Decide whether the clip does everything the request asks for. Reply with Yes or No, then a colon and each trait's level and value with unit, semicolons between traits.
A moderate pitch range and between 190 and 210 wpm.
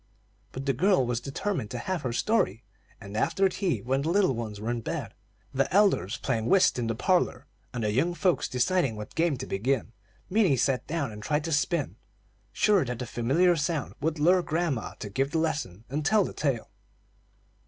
No: wide, 6.7 semitones; average, 195 wpm